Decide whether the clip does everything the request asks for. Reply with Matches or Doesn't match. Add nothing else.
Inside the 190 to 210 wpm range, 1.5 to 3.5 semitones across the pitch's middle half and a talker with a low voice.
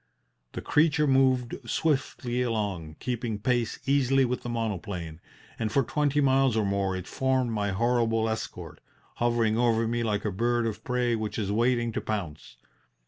Doesn't match